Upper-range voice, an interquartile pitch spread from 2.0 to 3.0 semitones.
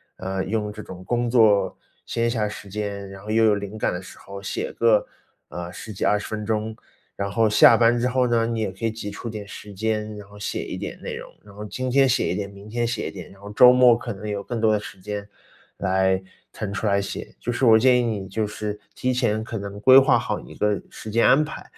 No: low, 105 Hz; narrow, 2.6 semitones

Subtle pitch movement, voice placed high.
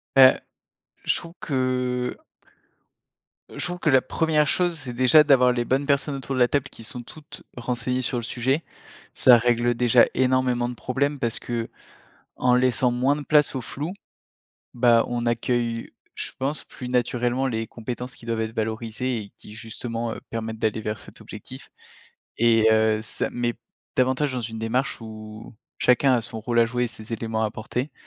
No: narrow, 2.2 semitones; low, 120 Hz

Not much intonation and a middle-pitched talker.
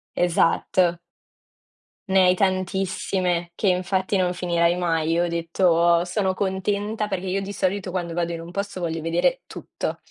Yes: narrow, 2.0 semitones; medium, 180 Hz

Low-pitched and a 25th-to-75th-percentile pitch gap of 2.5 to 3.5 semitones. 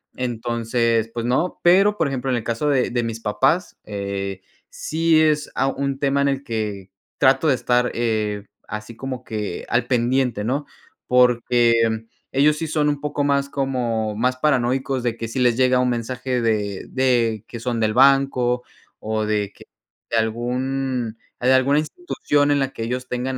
Yes: low, 125 Hz; average, 3.0 semitones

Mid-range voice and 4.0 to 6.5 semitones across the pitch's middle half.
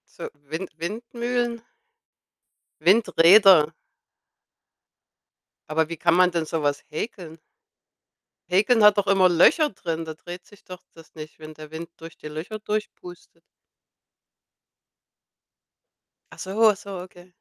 Yes: medium, 180 Hz; average, 4.5 semitones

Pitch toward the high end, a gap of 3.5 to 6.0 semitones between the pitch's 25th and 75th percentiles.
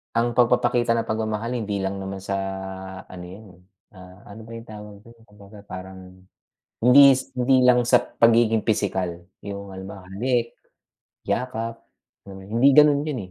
No: low, 110 Hz; average, 3.8 semitones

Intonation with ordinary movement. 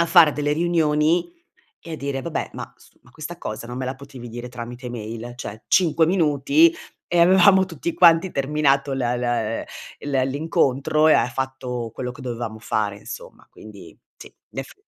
Yes: average, 5.0 semitones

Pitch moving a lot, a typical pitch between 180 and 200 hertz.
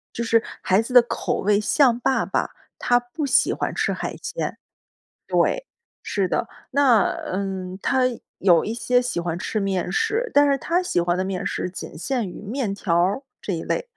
No: wide, 5.7 semitones; high, 220 Hz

